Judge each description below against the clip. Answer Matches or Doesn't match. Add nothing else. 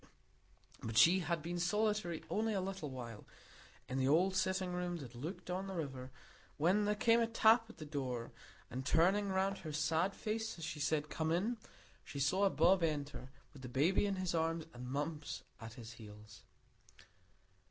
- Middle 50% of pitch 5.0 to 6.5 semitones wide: Matches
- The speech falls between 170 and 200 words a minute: Matches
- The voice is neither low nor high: Matches